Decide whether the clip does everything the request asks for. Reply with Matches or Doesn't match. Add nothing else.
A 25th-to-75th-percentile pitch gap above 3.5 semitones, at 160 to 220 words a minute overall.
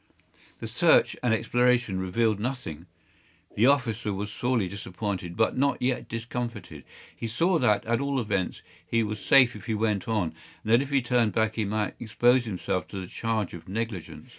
Doesn't match